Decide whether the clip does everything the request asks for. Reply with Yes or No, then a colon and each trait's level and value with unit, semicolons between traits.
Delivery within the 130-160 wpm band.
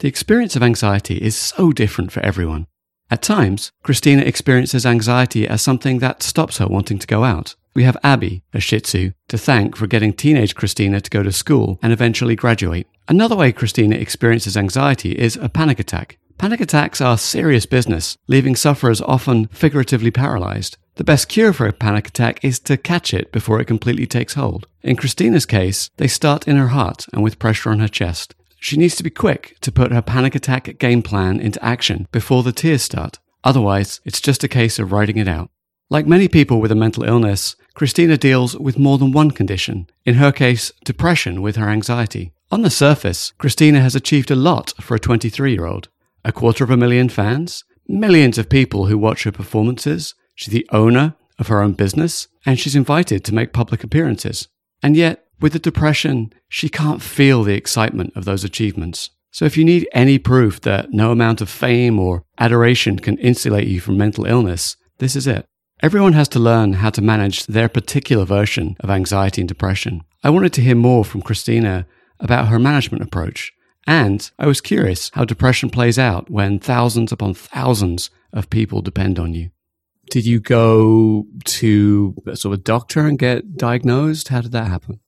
No: average, 190 wpm